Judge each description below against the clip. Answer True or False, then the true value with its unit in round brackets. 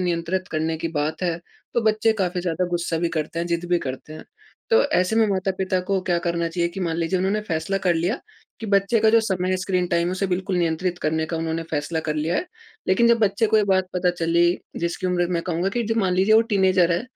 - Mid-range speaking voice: True (180 Hz)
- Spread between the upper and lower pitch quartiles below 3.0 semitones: True (2.5 semitones)